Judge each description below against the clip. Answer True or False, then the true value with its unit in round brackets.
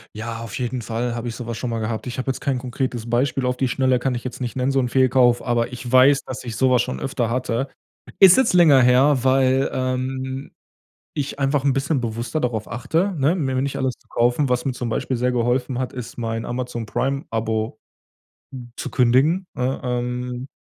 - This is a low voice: True (125 Hz)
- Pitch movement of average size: False (1.9 semitones)